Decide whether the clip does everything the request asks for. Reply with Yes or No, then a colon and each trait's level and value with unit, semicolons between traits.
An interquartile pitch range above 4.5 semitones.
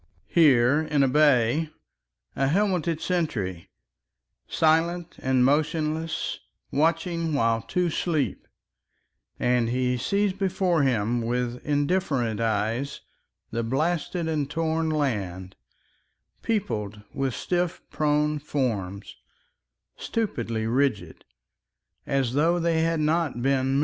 Yes: average, 5.3 semitones